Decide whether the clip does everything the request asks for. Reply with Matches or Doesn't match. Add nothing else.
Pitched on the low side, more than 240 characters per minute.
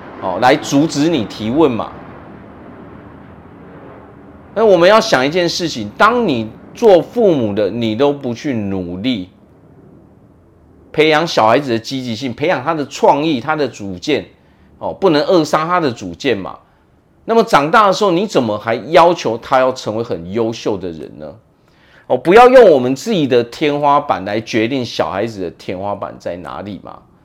Doesn't match